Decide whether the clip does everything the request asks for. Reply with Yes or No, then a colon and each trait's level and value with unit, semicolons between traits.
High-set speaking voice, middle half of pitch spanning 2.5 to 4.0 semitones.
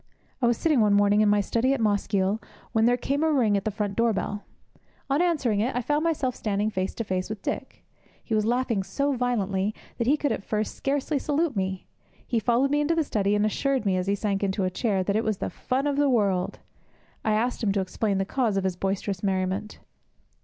No: high, 215 Hz; average, 4.5 semitones